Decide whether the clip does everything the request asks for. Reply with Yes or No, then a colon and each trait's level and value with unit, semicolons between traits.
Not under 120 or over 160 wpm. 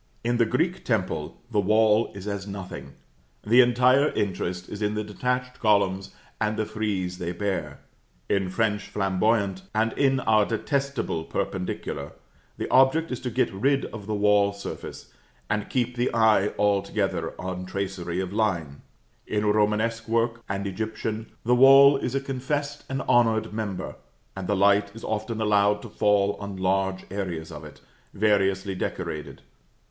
Yes: average, 155 wpm